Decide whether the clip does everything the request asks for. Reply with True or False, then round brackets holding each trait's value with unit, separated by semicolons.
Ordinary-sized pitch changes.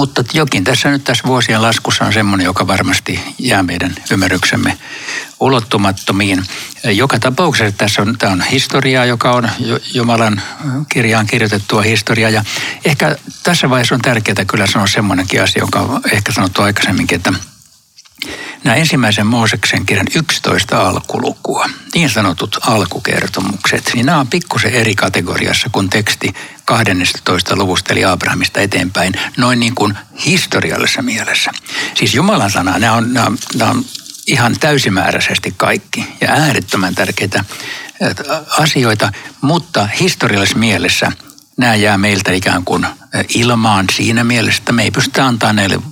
True (4.2 semitones)